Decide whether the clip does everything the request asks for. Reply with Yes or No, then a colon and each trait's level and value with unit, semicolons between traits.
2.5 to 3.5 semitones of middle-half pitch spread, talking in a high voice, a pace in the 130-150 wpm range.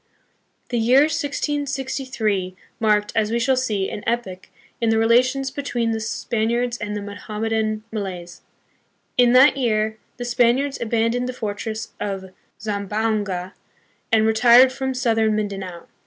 Yes: average, 2.9 semitones; high, 225 Hz; average, 140 wpm